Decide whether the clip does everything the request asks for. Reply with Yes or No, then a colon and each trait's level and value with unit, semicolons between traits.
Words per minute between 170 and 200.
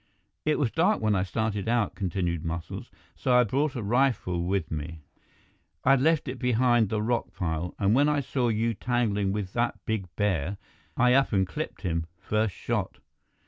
Yes: average, 185 wpm